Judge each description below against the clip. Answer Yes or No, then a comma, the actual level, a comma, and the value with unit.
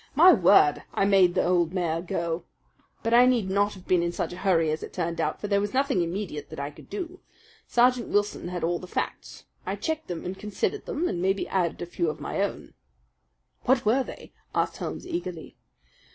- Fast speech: Yes, fast, 210 wpm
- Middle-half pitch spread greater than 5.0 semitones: Yes, wide, 5.6 semitones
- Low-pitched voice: No, high, 190 Hz